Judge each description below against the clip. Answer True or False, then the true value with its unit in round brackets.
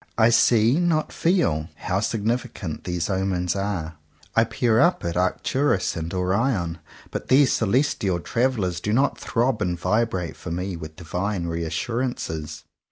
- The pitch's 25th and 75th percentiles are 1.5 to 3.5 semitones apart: False (5.4 semitones)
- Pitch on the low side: True (95 Hz)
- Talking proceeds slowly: False (145 wpm)